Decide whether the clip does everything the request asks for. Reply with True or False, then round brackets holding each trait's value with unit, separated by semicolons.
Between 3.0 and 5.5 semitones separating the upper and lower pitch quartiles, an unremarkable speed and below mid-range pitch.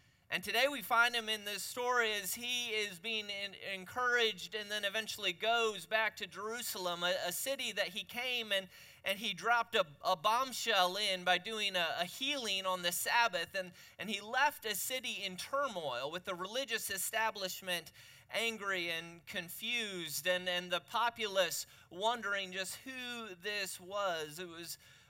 False (4.1 semitones; 165 wpm; 205 Hz)